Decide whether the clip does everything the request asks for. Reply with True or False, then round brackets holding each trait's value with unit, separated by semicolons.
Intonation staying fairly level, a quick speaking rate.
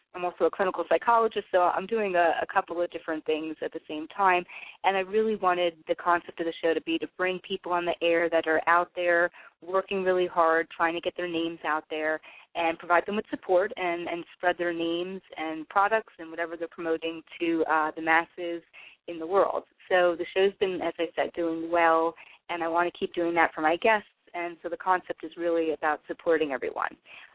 True (1.7 semitones; 220 wpm)